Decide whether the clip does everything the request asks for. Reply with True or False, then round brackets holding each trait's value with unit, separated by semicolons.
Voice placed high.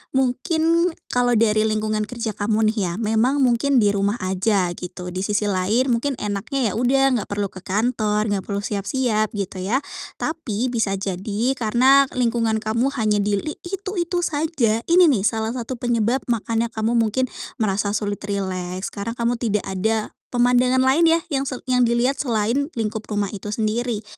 True (225 Hz)